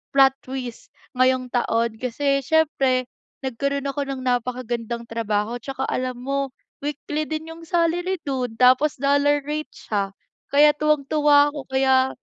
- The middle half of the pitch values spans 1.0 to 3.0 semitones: Yes, average, 2.7 semitones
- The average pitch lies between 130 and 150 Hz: No, very high, 270 Hz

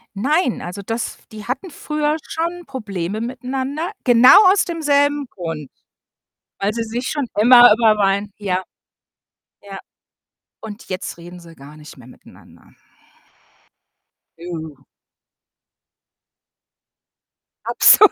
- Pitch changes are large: Yes, wide, 7.3 semitones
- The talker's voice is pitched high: Yes, high, 225 Hz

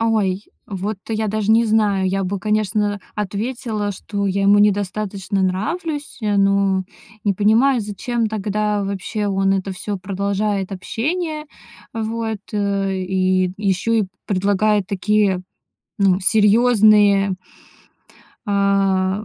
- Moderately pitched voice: No, high, 205 Hz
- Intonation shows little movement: Yes, narrow, 1.8 semitones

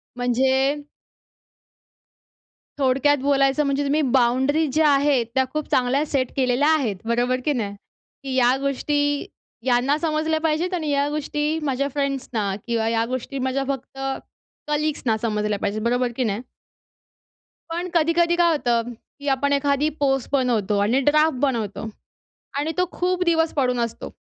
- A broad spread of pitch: No, average, 3.3 semitones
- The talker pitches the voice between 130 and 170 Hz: No, very high, 275 Hz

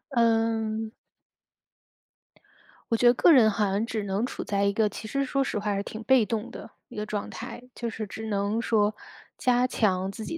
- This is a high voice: Yes, high, 220 Hz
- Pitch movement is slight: Yes, narrow, 2.2 semitones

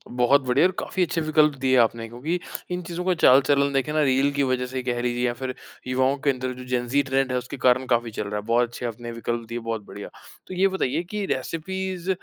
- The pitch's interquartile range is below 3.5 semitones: No, average, 3.8 semitones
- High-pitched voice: No, low, 130 Hz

